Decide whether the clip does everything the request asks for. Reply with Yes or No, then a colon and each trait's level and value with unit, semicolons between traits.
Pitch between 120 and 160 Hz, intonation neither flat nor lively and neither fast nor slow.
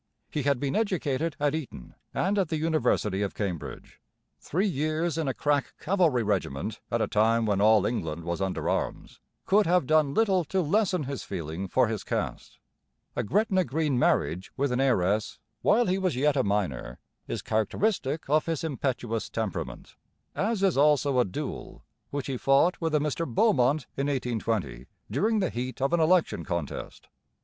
No: medium, 140 Hz; wide, 7.0 semitones; average, 175 wpm